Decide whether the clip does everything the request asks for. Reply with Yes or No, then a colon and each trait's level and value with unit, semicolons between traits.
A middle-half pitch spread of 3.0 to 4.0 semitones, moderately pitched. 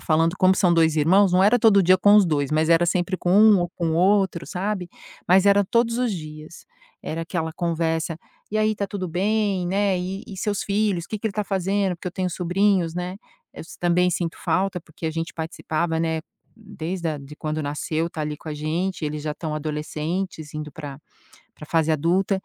Yes: average, 3.5 semitones; medium, 175 Hz